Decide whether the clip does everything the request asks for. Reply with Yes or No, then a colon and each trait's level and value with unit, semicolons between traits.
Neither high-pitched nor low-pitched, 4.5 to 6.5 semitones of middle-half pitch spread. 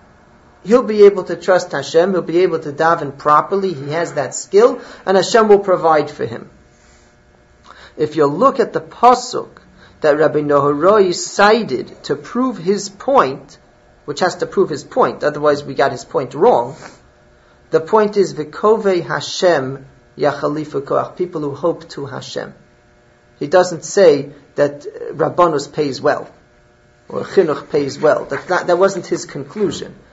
Yes: medium, 175 Hz; average, 5.1 semitones